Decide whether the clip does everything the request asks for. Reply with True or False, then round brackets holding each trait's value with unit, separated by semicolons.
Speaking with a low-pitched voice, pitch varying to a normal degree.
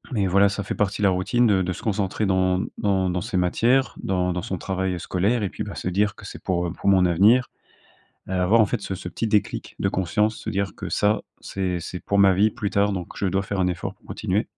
False (95 Hz; 2.2 semitones)